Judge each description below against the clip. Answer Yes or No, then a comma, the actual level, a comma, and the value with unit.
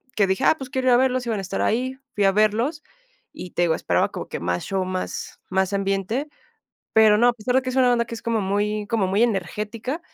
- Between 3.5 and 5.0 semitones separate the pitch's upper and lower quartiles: Yes, average, 4.1 semitones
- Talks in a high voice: Yes, high, 215 Hz